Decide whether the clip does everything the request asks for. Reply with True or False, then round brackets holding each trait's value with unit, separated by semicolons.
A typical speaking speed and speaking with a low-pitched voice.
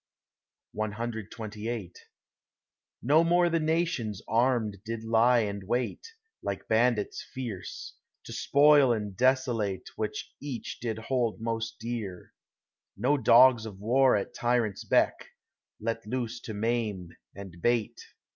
False (115 wpm; 115 Hz)